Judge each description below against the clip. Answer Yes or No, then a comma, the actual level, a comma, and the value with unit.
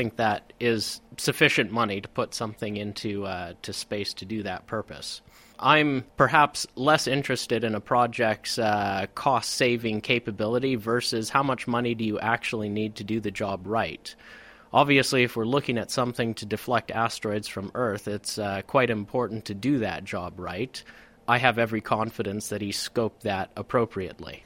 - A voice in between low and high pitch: No, low, 115 Hz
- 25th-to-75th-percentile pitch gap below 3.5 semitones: Yes, average, 3.0 semitones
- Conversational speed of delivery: Yes, average, 170 wpm